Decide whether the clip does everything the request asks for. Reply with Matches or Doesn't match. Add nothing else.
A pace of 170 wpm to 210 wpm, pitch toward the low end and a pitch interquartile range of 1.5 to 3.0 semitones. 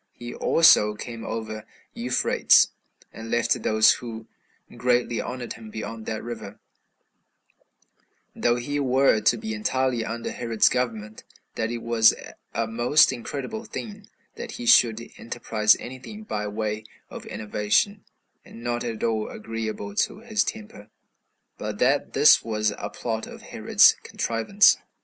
Doesn't match